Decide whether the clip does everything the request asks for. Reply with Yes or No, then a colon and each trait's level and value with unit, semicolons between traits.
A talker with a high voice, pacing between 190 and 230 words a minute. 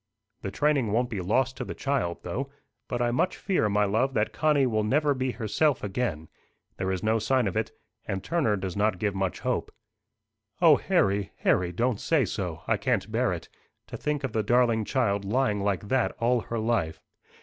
No: low, 110 Hz; average, 195 wpm